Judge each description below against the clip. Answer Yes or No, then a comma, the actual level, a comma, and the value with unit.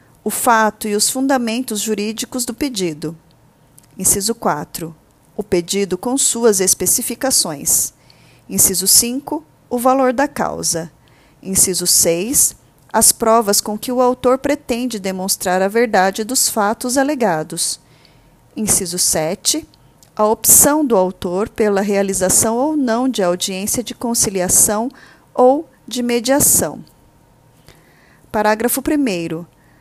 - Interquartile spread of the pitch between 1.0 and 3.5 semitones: No, wide, 5.4 semitones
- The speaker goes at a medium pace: No, slow, 110 wpm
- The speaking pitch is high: Yes, high, 215 Hz